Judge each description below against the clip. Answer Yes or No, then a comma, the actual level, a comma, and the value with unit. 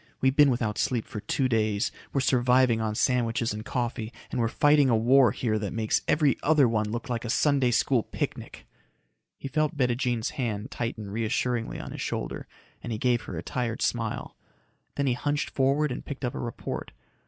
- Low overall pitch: Yes, low, 120 Hz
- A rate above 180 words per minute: Yes, average, 190 wpm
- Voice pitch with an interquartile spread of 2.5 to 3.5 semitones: Yes, average, 3.1 semitones